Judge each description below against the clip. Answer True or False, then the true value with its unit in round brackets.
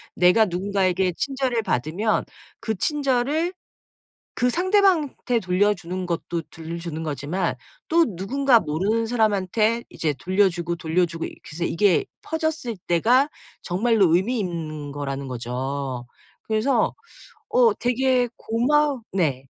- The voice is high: True (195 Hz)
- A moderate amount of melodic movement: False (6.7 semitones)